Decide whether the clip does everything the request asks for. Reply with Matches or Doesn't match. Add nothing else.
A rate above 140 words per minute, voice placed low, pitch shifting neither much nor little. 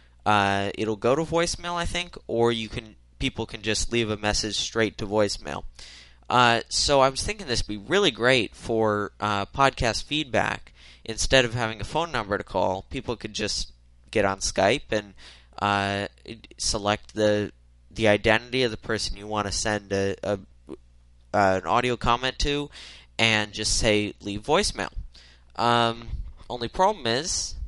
Matches